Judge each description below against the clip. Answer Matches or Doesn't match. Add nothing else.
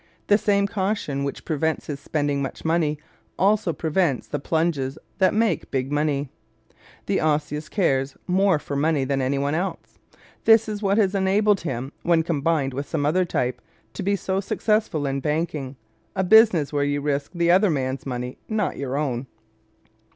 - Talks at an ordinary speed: Matches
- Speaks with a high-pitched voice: Doesn't match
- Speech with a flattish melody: Doesn't match